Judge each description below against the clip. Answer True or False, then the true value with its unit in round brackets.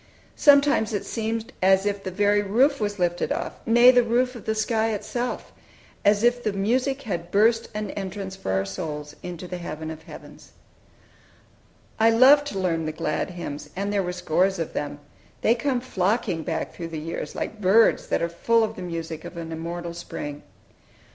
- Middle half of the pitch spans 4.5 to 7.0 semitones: True (5.1 semitones)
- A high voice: True (195 Hz)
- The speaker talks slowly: False (185 wpm)